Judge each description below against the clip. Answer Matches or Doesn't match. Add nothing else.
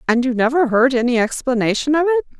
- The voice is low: Doesn't match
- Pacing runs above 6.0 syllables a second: Matches